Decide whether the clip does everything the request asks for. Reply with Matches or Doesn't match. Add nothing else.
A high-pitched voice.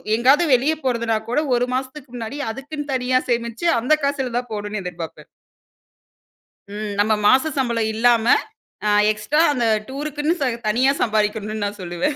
Matches